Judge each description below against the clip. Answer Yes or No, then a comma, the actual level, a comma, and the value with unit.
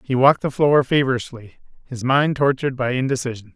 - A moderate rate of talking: Yes, average, 170 wpm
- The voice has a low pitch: Yes, low, 130 Hz